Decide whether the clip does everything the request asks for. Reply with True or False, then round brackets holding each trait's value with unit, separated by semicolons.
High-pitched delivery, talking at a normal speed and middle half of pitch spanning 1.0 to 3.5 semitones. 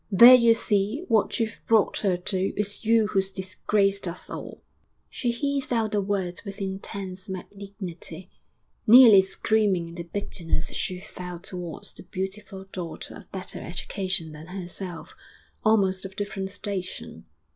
True (195 Hz; 145 wpm; 2.5 semitones)